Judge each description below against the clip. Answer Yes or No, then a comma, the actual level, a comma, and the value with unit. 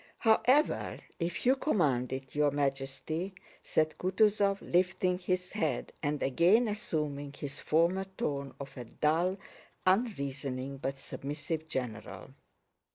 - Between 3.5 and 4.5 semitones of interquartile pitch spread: No, average, 5.3 semitones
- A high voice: No, medium, 155 Hz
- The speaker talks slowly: Yes, slow, 115 wpm